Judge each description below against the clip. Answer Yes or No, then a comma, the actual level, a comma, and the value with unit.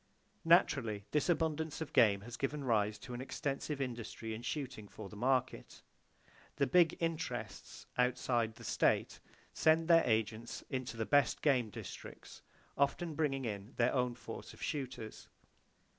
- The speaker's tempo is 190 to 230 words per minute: No, average, 145 wpm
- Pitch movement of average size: Yes, average, 4.7 semitones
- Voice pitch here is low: Yes, low, 125 Hz